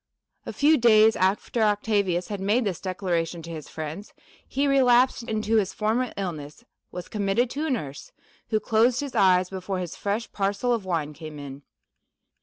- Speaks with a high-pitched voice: Yes, high, 200 Hz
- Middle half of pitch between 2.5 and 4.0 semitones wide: No, average, 4.5 semitones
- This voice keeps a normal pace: Yes, average, 170 wpm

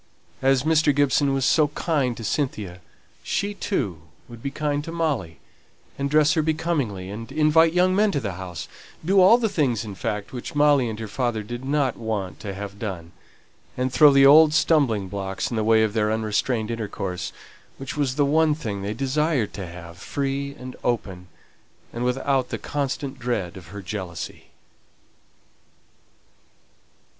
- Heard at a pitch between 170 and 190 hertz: No, low, 125 Hz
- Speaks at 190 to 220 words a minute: No, average, 170 wpm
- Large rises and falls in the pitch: Yes, wide, 6.1 semitones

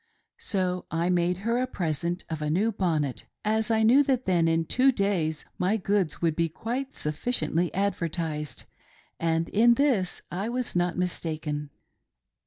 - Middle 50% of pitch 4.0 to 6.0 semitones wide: Yes, average, 5.2 semitones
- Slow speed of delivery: No, average, 155 wpm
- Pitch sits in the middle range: Yes, medium, 180 Hz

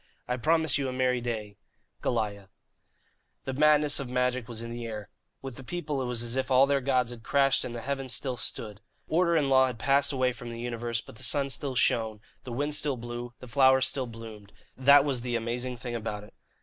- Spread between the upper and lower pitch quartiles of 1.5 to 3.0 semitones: Yes, average, 2.7 semitones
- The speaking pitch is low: Yes, low, 125 Hz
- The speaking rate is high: Yes, fast, 220 wpm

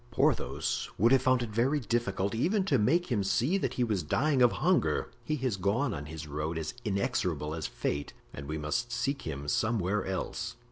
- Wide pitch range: Yes, wide, 7.9 semitones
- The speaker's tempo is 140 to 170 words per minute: No, average, 195 wpm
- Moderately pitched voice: No, low, 110 Hz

